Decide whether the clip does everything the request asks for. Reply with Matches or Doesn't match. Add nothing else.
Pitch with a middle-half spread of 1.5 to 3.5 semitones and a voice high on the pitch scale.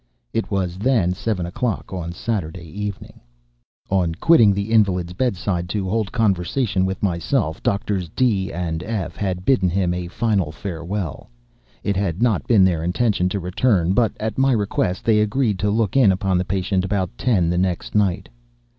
Doesn't match